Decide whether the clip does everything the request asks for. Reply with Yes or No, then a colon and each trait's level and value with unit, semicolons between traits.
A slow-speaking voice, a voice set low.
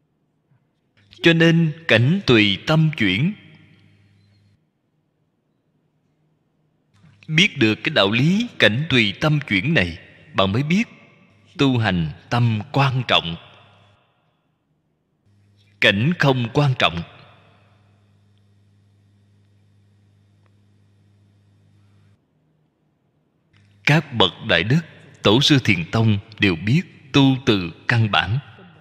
Yes: slow, 85 wpm; low, 115 Hz